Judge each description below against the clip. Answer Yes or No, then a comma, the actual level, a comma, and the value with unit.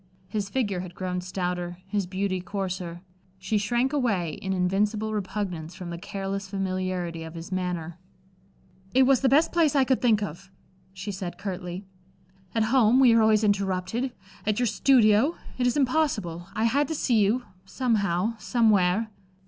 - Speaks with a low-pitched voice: No, high, 200 Hz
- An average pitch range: Yes, average, 4.2 semitones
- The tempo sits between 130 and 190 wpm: Yes, average, 160 wpm